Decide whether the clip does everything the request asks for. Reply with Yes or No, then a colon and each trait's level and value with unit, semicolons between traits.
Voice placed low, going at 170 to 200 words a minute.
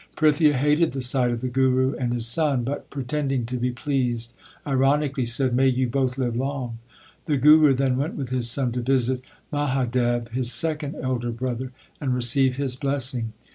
Yes: low, 130 Hz; average, 180 wpm